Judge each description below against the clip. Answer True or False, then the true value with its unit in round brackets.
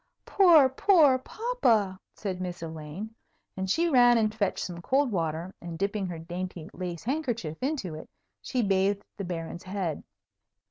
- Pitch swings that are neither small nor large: False (6.5 semitones)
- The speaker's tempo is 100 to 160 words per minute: True (150 wpm)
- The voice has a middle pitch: False (195 Hz)